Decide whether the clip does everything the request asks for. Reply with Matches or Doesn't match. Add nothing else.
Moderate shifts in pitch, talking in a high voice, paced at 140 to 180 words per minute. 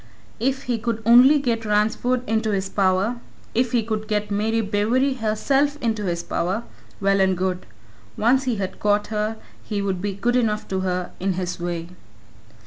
Matches